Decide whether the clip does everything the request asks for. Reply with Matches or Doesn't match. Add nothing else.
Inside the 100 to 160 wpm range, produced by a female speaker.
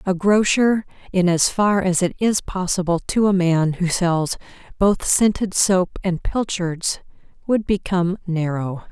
Matches